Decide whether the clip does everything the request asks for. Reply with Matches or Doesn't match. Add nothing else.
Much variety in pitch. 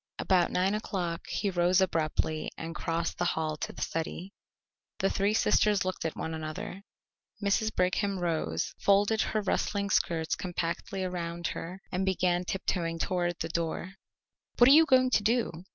Doesn't match